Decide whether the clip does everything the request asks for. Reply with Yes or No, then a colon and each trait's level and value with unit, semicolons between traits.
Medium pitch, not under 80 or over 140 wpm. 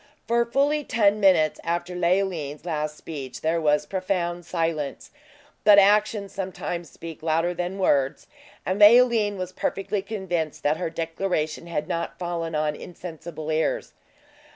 Yes: medium, 175 Hz; slow, 135 wpm